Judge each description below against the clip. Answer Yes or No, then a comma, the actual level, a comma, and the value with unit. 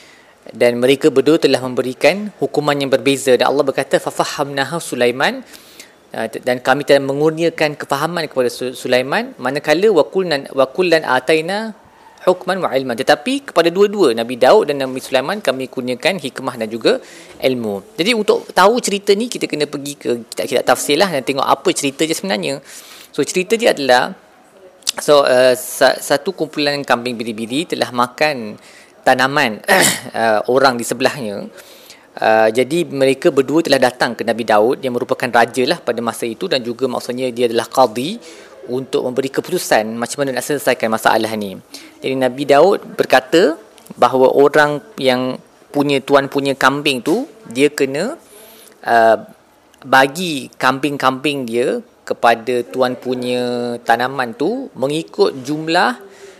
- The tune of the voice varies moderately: Yes, average, 3.8 semitones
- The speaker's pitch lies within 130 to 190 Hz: Yes, low, 135 Hz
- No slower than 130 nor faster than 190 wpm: Yes, average, 140 wpm